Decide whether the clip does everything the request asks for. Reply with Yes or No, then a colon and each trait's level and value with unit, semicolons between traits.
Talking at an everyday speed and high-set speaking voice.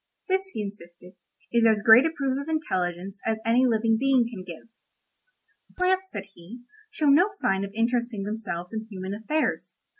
Yes: average, 170 wpm; high, 225 Hz